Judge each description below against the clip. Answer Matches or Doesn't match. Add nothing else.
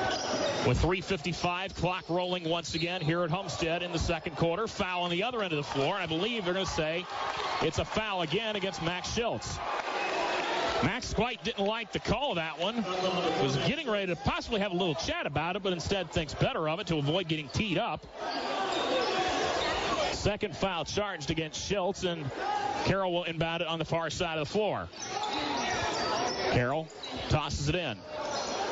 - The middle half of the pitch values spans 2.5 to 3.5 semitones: Matches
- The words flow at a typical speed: Matches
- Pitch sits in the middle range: Matches